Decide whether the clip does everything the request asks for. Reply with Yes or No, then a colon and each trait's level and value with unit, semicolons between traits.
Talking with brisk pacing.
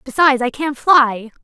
No: average, 165 wpm